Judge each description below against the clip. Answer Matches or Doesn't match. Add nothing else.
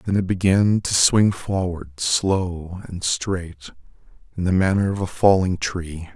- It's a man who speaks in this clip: Matches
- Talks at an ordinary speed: Matches